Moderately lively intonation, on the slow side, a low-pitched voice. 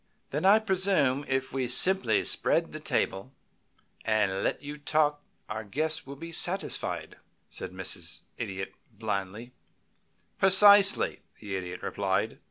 No: wide, 8.4 semitones; slow, 125 wpm; low, 130 Hz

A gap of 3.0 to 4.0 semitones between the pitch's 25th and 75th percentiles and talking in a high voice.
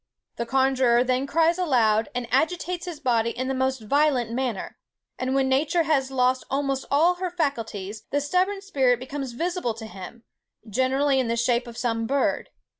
Yes: average, 3.5 semitones; very high, 265 Hz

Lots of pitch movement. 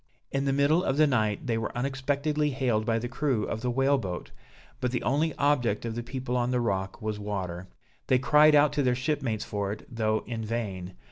No: average, 4.3 semitones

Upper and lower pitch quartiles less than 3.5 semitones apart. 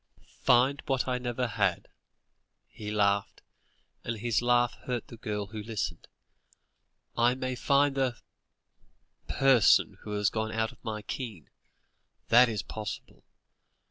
Yes: average, 2.9 semitones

